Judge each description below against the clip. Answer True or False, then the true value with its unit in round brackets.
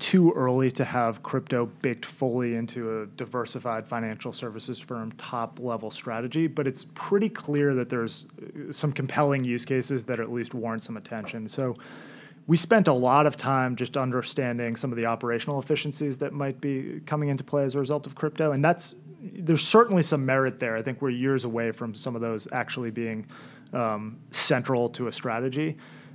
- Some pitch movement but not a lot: True (3.5 semitones)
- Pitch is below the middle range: True (130 Hz)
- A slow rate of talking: False (185 wpm)